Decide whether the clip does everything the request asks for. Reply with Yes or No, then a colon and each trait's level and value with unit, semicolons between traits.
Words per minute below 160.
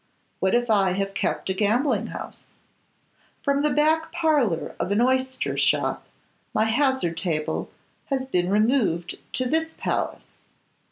Yes: slow, 135 wpm